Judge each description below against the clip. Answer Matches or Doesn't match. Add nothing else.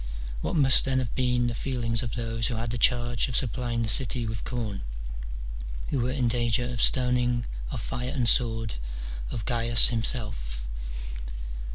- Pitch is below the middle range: Matches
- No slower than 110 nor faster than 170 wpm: Matches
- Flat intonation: Matches